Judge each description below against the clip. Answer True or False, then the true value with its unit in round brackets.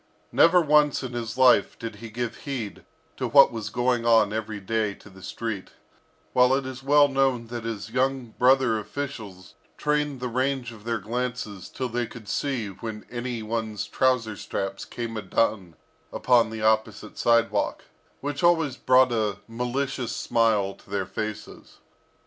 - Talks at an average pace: True (160 wpm)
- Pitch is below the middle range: True (115 Hz)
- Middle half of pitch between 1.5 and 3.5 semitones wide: True (3.1 semitones)